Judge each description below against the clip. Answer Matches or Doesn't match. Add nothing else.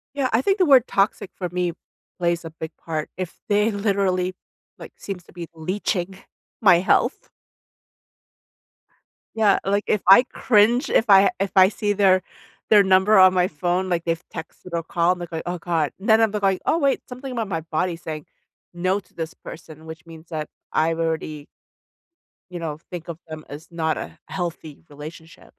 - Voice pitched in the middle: Matches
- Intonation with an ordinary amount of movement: Matches